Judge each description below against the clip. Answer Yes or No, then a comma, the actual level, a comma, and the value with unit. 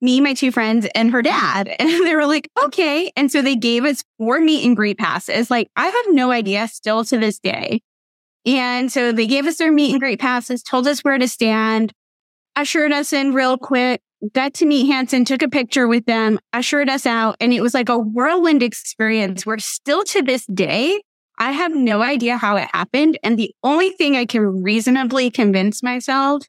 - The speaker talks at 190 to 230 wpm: Yes, fast, 205 wpm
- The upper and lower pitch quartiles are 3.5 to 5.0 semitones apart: Yes, average, 4.0 semitones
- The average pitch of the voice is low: No, very high, 255 Hz